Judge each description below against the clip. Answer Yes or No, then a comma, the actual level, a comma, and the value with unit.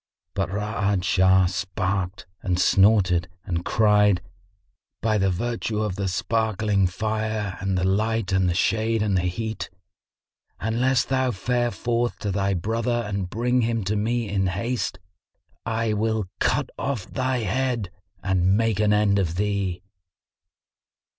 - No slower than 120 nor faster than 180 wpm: Yes, average, 140 wpm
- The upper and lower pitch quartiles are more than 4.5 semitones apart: No, average, 3.1 semitones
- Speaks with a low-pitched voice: Yes, low, 105 Hz